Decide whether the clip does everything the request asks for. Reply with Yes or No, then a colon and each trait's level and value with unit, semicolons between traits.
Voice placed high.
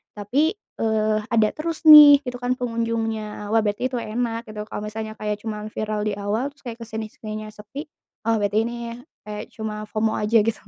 Yes: high, 220 Hz